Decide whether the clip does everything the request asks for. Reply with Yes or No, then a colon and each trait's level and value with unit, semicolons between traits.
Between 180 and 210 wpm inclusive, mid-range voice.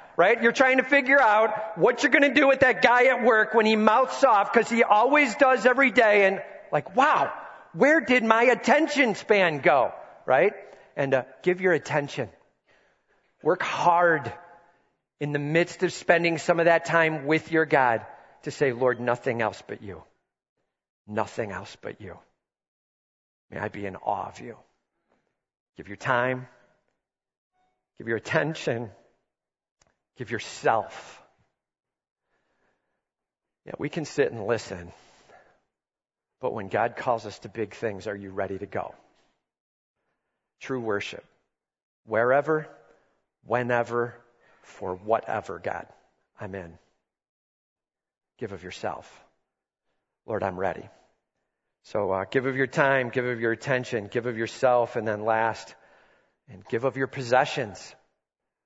No: average, 140 wpm; medium, 155 Hz